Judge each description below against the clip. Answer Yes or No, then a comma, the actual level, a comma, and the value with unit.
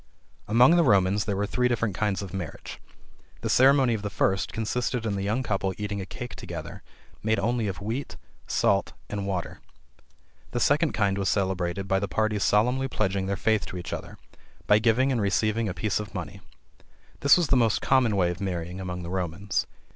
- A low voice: Yes, low, 105 Hz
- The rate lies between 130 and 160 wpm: No, average, 195 wpm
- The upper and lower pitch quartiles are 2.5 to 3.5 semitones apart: Yes, average, 3.2 semitones